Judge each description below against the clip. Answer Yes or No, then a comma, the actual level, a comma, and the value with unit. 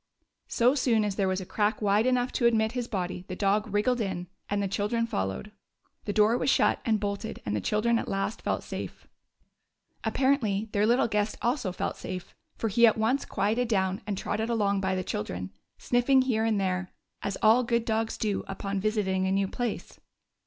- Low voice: No, high, 210 Hz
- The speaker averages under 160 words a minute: No, average, 195 wpm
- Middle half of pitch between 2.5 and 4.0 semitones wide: Yes, average, 3.0 semitones